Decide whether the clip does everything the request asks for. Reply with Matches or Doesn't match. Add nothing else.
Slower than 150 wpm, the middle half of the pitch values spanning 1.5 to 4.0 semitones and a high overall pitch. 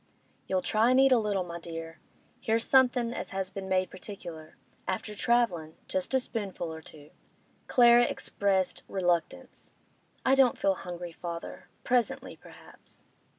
Doesn't match